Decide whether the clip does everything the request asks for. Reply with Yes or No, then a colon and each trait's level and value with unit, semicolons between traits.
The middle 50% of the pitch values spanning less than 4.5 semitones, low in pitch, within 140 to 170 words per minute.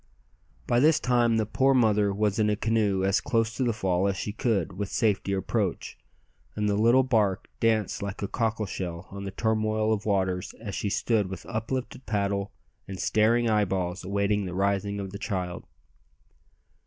No: narrow, 2.4 semitones; low, 105 Hz; average, 180 wpm